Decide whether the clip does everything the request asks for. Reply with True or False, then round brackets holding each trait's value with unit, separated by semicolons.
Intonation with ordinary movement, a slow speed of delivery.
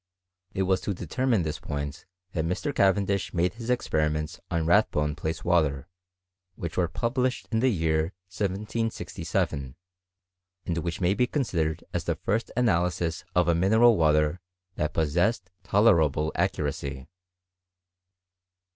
True (4.8 semitones; 125 wpm)